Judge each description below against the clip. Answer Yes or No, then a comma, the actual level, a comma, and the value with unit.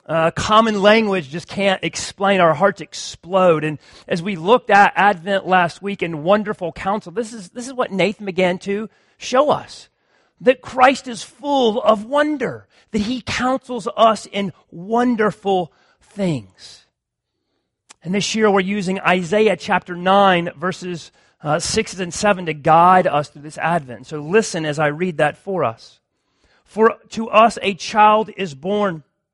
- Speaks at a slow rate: No, average, 160 wpm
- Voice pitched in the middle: No, high, 195 Hz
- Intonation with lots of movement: No, average, 3.7 semitones